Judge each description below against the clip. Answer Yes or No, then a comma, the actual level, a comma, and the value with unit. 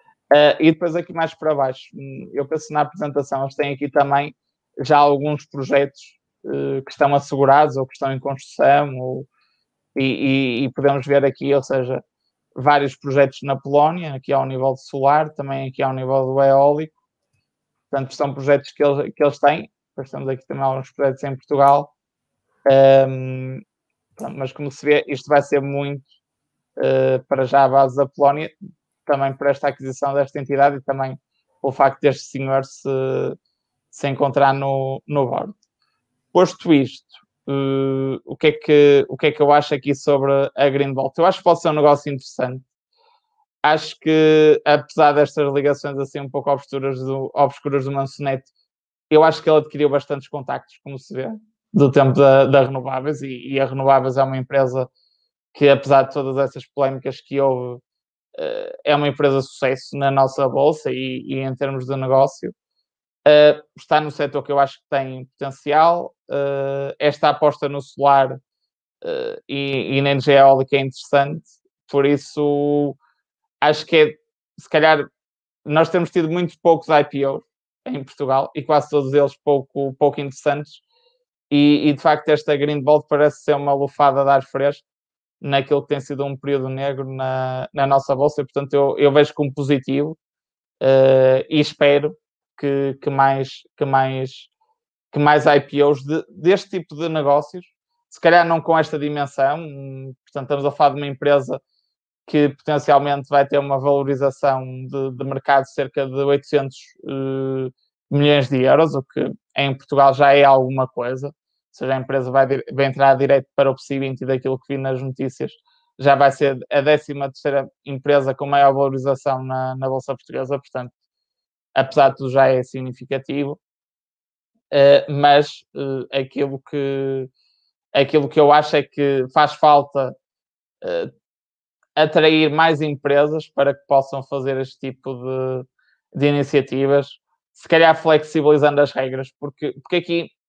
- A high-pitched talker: No, medium, 140 Hz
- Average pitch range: No, narrow, 1.5 semitones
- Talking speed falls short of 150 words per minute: No, average, 165 wpm